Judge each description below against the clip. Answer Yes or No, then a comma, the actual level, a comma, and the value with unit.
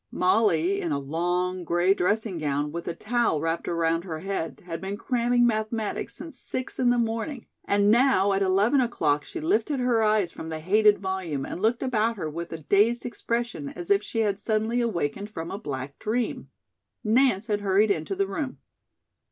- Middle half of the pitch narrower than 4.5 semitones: No, average, 5.2 semitones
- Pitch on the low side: No, high, 200 Hz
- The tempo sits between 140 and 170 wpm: No, average, 185 wpm